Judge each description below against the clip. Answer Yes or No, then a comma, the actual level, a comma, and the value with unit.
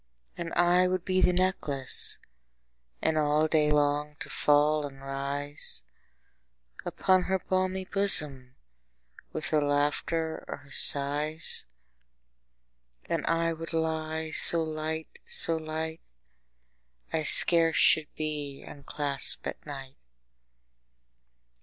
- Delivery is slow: Yes, slow, 110 wpm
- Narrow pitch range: Yes, narrow, 2.3 semitones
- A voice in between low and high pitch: Yes, medium, 155 Hz